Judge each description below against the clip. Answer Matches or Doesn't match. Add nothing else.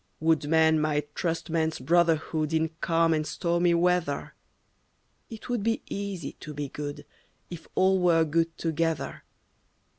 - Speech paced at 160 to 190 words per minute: Doesn't match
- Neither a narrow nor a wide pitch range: Doesn't match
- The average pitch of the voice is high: Doesn't match